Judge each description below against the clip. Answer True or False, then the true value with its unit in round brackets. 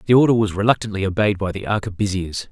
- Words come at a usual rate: True (190 wpm)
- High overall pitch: False (100 Hz)